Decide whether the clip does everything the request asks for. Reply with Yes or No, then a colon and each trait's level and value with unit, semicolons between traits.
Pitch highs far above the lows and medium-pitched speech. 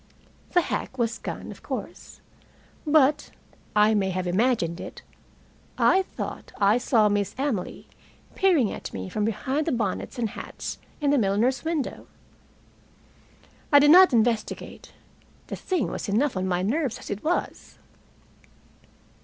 No: wide, 6.1 semitones; high, 235 Hz